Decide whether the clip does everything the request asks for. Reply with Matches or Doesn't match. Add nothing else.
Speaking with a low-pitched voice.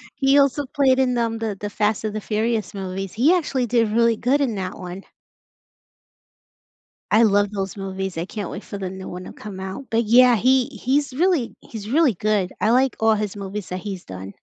Doesn't match